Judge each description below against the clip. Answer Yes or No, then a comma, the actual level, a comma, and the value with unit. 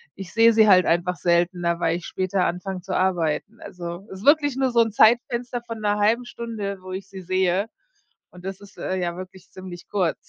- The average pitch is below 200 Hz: Yes, high, 190 Hz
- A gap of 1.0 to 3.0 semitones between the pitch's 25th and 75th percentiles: No, average, 3.7 semitones